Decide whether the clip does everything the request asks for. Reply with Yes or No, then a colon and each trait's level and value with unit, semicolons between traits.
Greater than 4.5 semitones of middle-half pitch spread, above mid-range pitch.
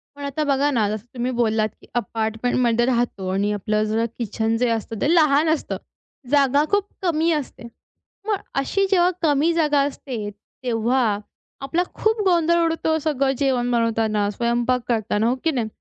Yes: average, 5.2 semitones; very high, 250 Hz